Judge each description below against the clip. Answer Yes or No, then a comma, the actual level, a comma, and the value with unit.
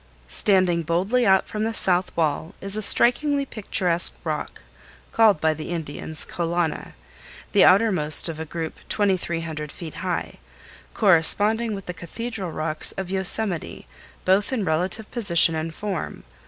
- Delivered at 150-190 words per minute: No, average, 140 wpm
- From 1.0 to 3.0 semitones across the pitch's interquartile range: No, average, 4.2 semitones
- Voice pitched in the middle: Yes, medium, 180 Hz